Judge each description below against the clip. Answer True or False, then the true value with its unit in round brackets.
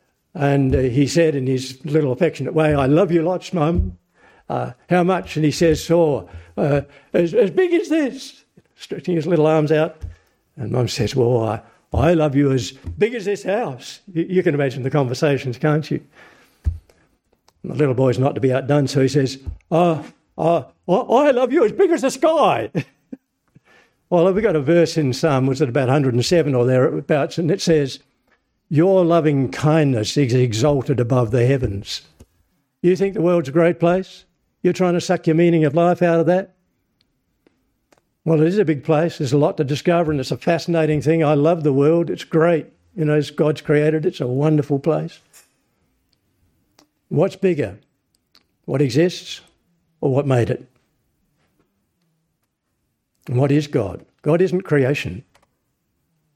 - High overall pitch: False (155 Hz)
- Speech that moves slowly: False (175 wpm)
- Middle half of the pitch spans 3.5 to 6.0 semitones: True (4.2 semitones)